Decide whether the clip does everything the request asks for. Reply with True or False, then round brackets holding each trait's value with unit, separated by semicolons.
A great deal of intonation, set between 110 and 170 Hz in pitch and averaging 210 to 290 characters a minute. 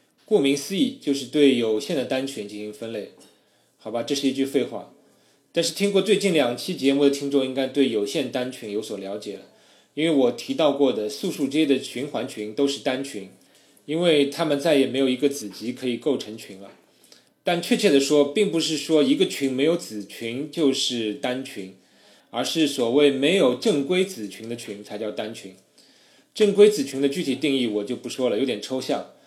False (5.0 semitones; 135 Hz; 285 characters per minute)